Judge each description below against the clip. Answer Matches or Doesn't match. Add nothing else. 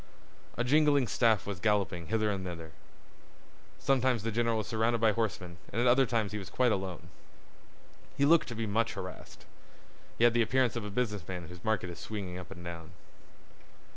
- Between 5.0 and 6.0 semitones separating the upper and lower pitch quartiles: Doesn't match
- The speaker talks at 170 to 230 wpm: Matches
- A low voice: Matches